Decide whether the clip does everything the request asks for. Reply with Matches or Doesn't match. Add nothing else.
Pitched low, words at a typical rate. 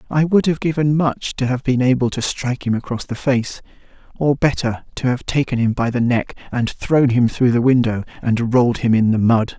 Doesn't match